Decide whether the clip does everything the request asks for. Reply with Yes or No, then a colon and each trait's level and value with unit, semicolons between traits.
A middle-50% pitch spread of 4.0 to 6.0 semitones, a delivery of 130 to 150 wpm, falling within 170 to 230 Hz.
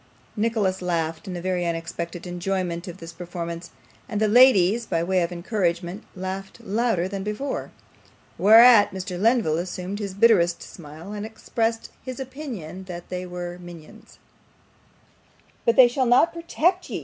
Yes: average, 4.4 semitones; average, 145 wpm; high, 190 Hz